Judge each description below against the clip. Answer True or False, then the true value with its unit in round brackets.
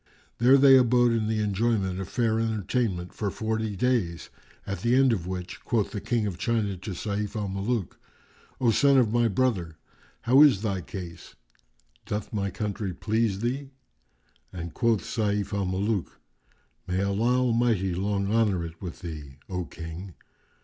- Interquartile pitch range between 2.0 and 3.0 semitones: False (3.7 semitones)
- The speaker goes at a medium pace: True (160 wpm)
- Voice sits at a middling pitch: False (105 Hz)